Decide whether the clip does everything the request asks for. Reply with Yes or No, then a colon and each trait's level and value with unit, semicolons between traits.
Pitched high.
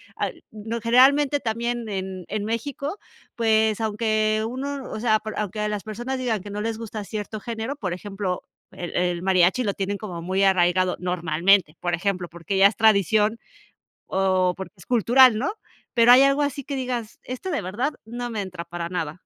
Yes: high, 215 Hz